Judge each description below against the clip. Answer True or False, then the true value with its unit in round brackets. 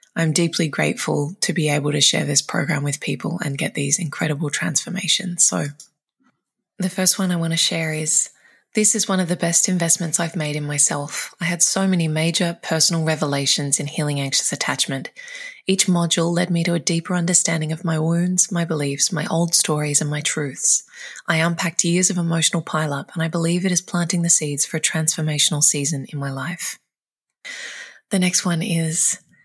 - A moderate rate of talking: True (190 wpm)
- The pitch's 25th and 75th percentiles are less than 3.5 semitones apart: True (2.8 semitones)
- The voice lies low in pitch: False (165 Hz)